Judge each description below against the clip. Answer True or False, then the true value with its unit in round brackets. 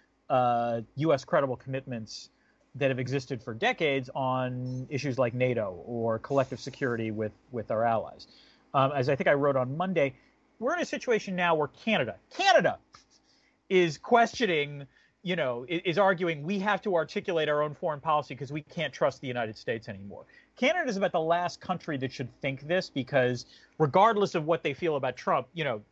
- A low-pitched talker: False (145 Hz)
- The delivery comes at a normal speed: True (185 wpm)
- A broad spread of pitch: True (6.1 semitones)